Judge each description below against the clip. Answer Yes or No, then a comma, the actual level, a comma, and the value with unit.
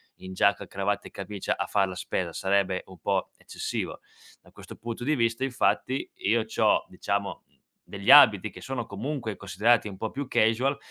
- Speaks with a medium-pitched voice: No, low, 105 Hz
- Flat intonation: No, average, 3.3 semitones